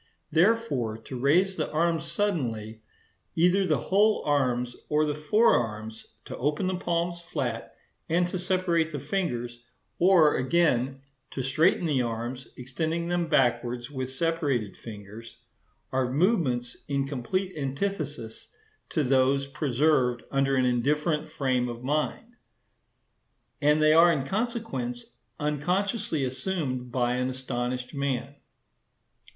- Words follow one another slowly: Yes, slow, 120 wpm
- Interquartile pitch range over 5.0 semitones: Yes, wide, 5.4 semitones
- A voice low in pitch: No, medium, 145 Hz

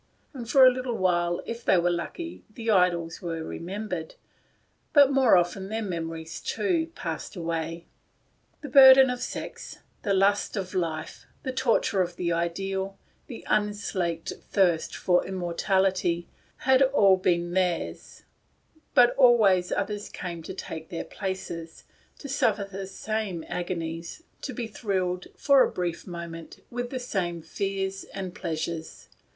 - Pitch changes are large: No, average, 4.3 semitones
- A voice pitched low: No, high, 190 Hz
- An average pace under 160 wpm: Yes, average, 145 wpm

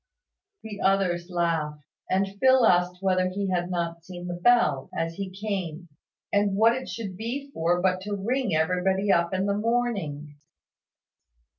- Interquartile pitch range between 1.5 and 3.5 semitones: Yes, average, 2.9 semitones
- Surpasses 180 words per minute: No, average, 155 wpm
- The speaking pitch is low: No, medium, 185 Hz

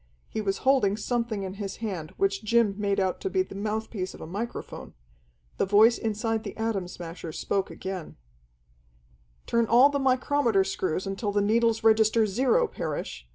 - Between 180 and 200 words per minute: No, average, 165 wpm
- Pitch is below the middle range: No, high, 210 Hz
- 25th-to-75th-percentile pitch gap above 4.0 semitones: No, average, 3.1 semitones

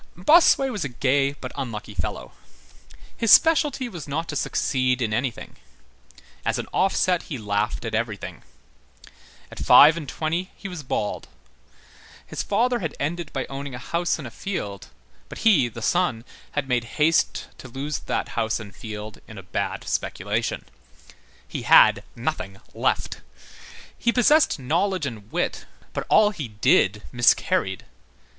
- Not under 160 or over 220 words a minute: No, average, 150 wpm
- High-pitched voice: No, medium, 140 Hz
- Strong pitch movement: Yes, wide, 7.6 semitones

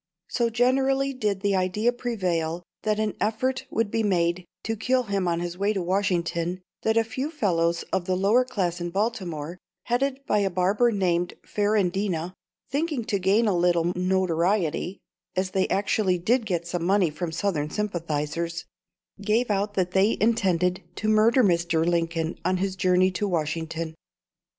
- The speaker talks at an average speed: Yes, average, 160 wpm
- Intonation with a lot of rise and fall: No, average, 3.9 semitones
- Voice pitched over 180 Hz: Yes, high, 190 Hz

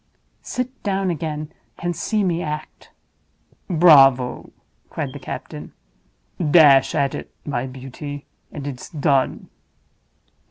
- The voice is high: No, medium, 150 Hz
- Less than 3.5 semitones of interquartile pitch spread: No, average, 4.3 semitones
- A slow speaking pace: Yes, slow, 105 wpm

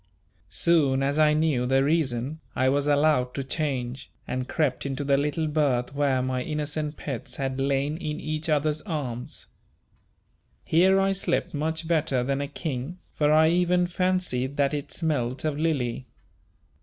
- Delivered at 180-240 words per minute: No, average, 155 wpm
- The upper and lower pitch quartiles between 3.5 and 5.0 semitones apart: No, average, 3.0 semitones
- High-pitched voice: No, medium, 145 Hz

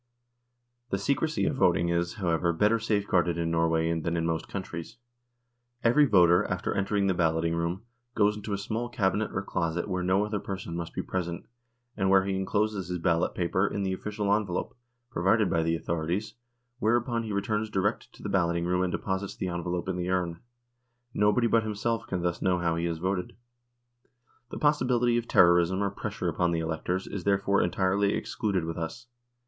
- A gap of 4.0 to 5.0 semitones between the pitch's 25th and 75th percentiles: No, average, 3.4 semitones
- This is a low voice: Yes, very low, 95 Hz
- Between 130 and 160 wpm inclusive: No, average, 185 wpm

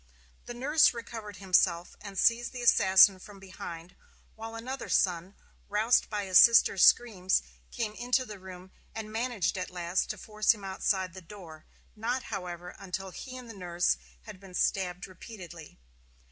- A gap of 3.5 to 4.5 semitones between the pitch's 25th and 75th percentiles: Yes, average, 3.8 semitones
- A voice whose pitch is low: No, high, 195 Hz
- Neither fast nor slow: Yes, average, 160 wpm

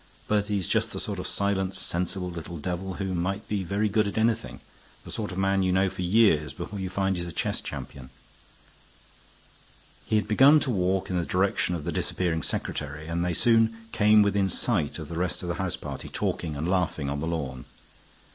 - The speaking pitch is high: No, very low, 95 Hz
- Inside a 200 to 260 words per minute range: Yes, fast, 205 wpm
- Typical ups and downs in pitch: Yes, average, 3.0 semitones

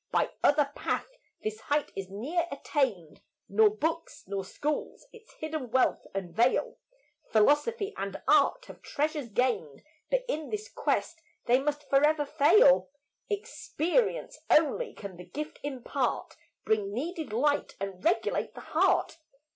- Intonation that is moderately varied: No, wide, 7.1 semitones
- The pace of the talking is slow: Yes, slow, 130 wpm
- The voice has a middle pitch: No, very high, 290 Hz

